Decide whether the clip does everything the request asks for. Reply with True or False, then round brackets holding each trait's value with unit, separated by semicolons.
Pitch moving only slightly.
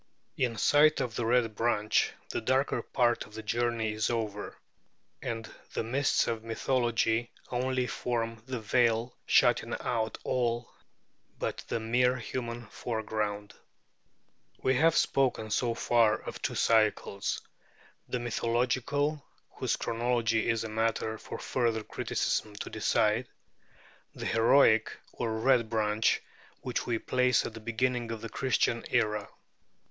True (2.0 semitones)